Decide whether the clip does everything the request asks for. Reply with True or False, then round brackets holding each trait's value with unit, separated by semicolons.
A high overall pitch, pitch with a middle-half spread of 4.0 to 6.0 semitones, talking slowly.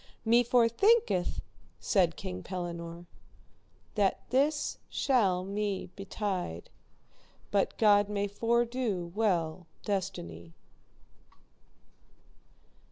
True (200 Hz; 4.7 semitones; 75 wpm)